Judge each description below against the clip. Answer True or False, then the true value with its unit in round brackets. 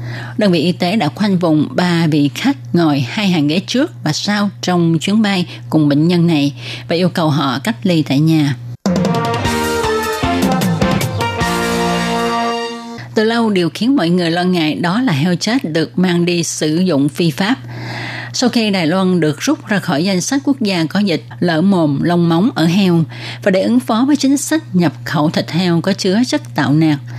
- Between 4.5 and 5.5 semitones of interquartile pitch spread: True (5.2 semitones)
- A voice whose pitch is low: False (175 Hz)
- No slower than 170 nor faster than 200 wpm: True (190 wpm)